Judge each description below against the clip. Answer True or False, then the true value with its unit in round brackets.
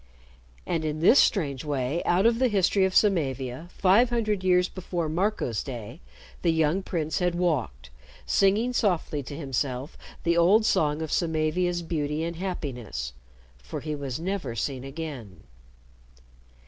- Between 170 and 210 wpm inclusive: False (145 wpm)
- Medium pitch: True (160 Hz)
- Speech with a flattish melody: False (5.1 semitones)